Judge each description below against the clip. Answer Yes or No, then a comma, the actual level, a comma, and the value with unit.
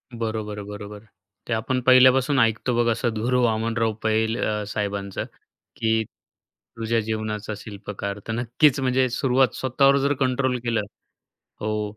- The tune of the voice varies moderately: Yes, average, 3.0 semitones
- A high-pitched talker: No, low, 115 Hz